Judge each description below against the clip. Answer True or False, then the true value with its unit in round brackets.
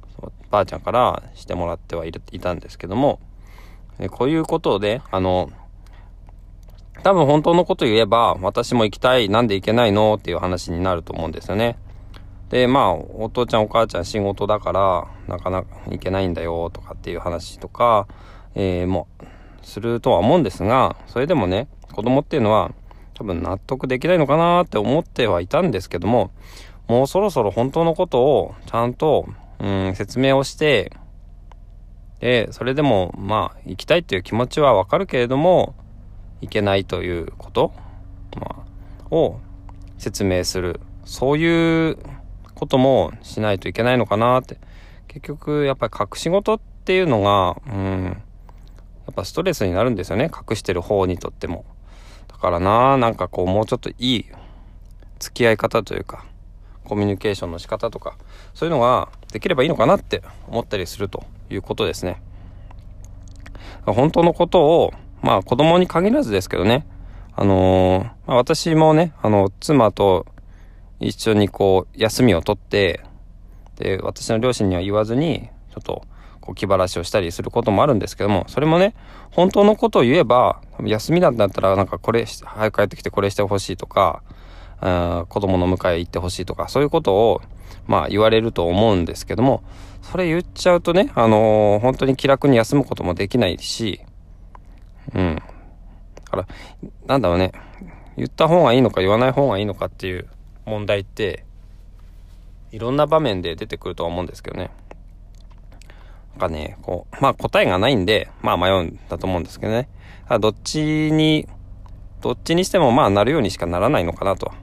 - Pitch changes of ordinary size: True (5.0 semitones)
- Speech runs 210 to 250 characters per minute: False (350 characters per minute)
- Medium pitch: False (100 Hz)